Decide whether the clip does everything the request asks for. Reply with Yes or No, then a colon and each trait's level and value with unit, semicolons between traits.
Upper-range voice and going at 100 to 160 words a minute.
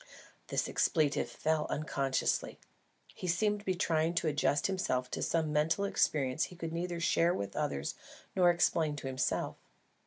No: medium, 160 Hz; average, 155 wpm